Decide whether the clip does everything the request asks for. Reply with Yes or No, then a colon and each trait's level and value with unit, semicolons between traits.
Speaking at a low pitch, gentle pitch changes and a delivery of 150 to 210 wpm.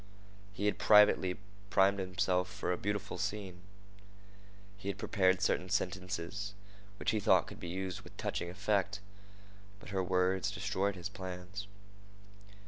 No: very low, 95 Hz; narrow, 1.7 semitones; slow, 135 wpm